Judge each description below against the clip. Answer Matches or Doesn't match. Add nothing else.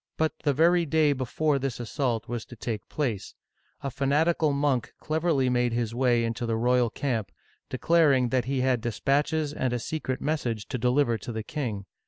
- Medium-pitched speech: Doesn't match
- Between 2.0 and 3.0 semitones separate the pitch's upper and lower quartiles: Doesn't match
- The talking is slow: Doesn't match